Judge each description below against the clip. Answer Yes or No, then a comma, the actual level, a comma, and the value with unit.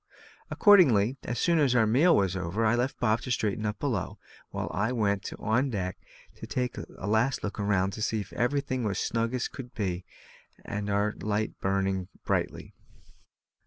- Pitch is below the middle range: Yes, low, 110 Hz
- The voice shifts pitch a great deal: No, average, 3.7 semitones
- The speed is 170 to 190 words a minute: Yes, average, 185 wpm